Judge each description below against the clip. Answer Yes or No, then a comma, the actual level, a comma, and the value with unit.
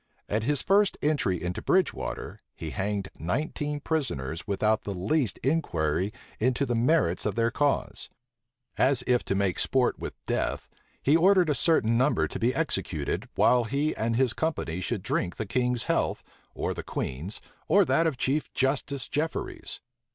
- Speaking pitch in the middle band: No, low, 125 Hz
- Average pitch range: No, wide, 7.0 semitones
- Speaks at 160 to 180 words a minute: Yes, average, 165 wpm